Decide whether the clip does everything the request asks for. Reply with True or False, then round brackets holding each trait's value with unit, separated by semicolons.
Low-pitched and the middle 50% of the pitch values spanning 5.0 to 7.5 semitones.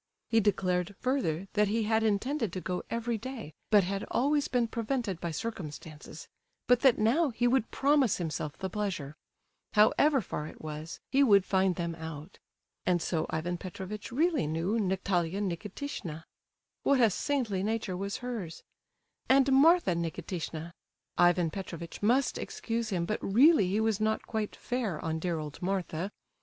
False (200 Hz; 5.4 semitones)